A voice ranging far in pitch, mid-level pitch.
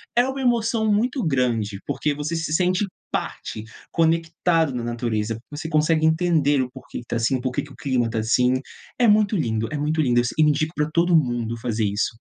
Yes: wide, 5.7 semitones; medium, 150 Hz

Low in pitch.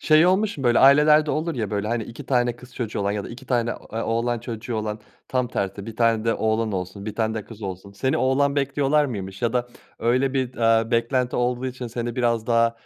Yes: low, 120 Hz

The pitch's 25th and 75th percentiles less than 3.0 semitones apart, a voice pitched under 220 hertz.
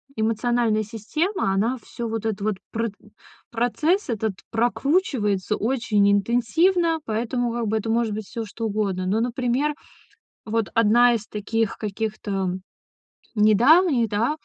No: narrow, 2.5 semitones; high, 225 Hz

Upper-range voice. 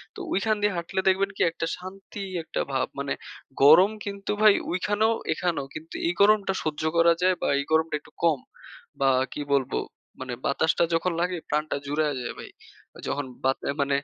No: medium, 170 Hz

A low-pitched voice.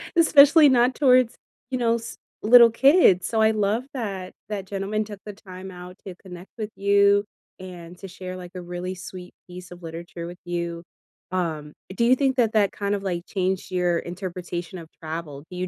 No: high, 190 Hz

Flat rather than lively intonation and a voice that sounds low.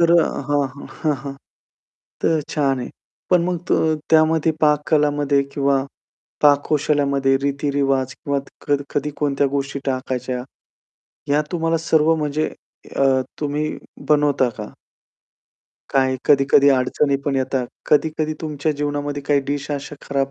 No: narrow, 1.7 semitones; medium, 145 Hz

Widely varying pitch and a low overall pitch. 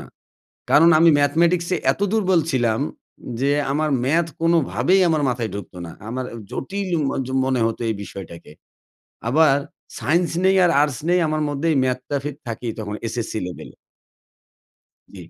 No: wide, 5.8 semitones; medium, 145 Hz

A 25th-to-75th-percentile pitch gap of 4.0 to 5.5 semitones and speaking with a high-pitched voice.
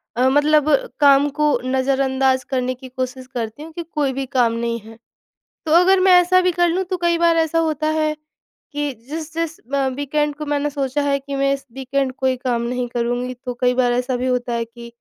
No: average, 3.3 semitones; very high, 275 Hz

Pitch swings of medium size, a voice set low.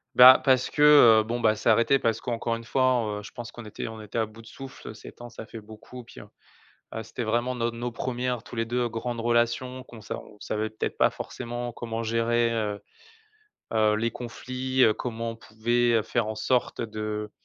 No: narrow, 1.7 semitones; low, 115 Hz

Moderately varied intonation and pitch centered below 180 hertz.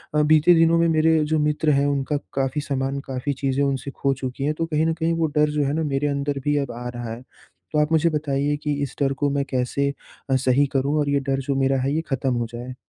No: narrow, 2.0 semitones; medium, 140 Hz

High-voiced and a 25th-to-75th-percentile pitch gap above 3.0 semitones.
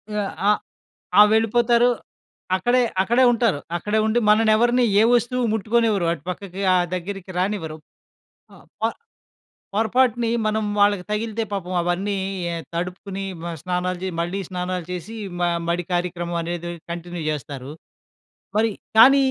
Yes: high, 200 Hz; average, 4.1 semitones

